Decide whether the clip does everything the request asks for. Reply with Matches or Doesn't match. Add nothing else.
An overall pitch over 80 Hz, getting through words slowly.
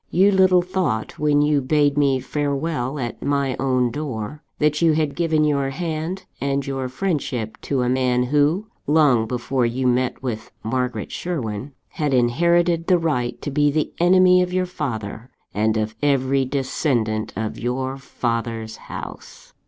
Doesn't match